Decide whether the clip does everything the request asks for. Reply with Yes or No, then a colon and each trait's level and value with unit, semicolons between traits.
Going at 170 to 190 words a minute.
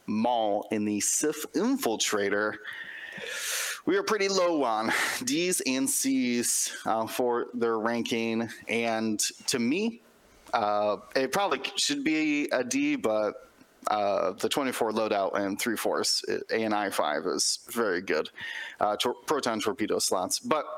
No: average, 140 wpm